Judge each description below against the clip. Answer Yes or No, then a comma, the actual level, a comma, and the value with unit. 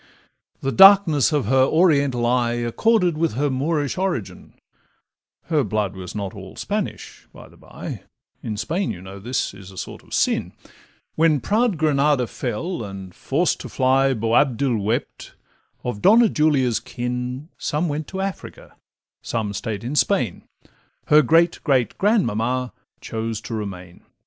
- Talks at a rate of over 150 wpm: No, average, 145 wpm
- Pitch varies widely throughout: Yes, wide, 5.8 semitones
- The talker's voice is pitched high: No, low, 130 Hz